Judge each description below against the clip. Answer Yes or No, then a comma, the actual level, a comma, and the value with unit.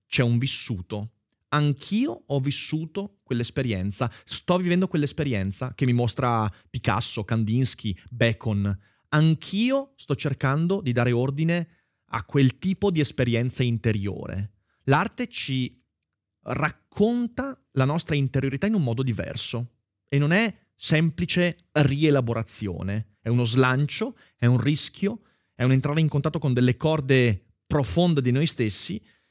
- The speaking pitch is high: No, low, 135 Hz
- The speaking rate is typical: Yes, average, 125 wpm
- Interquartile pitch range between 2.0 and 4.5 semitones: No, wide, 5.4 semitones